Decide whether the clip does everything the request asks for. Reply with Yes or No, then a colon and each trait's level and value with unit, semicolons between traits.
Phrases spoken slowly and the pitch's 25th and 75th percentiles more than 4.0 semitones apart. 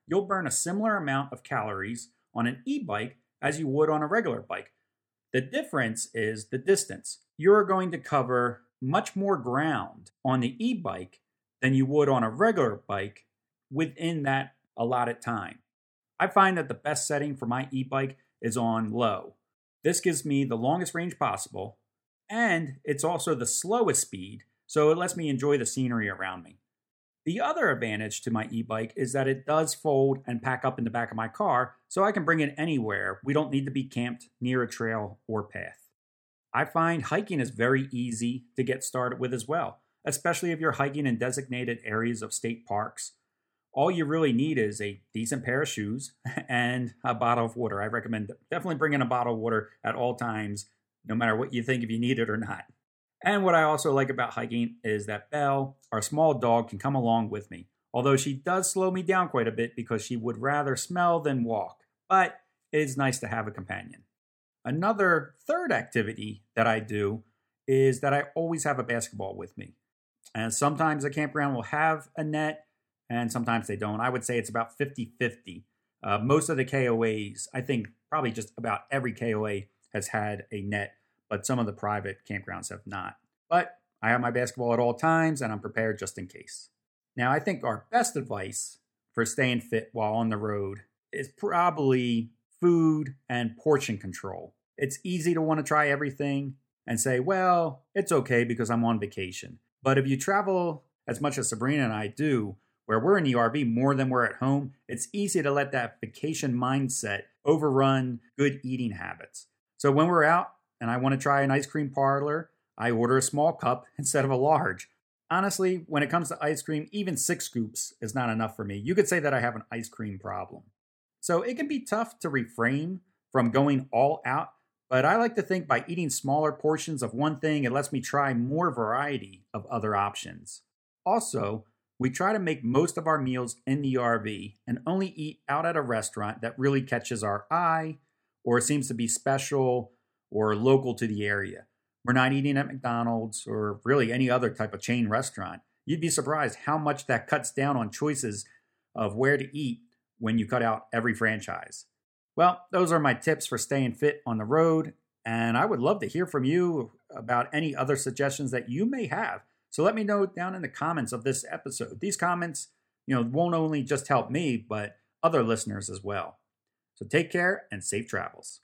No: average, 200 wpm; average, 4.8 semitones